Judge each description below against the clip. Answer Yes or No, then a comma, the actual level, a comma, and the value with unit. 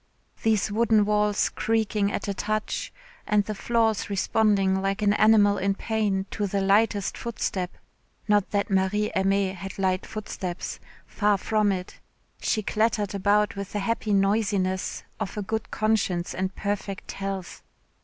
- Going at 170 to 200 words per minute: No, average, 145 wpm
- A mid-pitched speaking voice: No, high, 205 Hz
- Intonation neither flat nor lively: No, narrow, 1.7 semitones